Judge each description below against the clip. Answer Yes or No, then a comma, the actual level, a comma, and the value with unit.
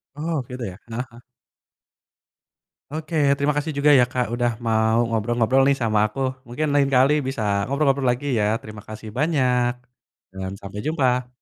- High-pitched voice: No, low, 125 Hz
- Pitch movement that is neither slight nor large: Yes, average, 3.9 semitones